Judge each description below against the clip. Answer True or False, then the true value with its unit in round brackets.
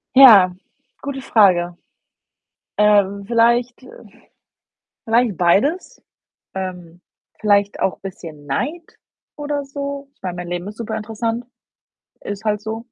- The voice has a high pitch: True (210 Hz)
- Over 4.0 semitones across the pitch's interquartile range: True (4.8 semitones)